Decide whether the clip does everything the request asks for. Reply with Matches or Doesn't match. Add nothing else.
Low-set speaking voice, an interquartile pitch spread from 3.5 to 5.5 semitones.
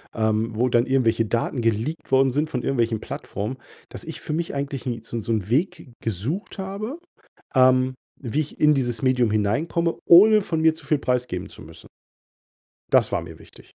Matches